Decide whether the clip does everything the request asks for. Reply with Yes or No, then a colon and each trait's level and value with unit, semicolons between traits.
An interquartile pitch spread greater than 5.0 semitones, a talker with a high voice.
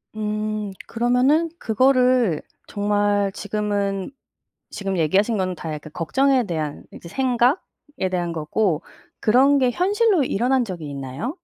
Yes: wide, 5.6 semitones; high, 210 Hz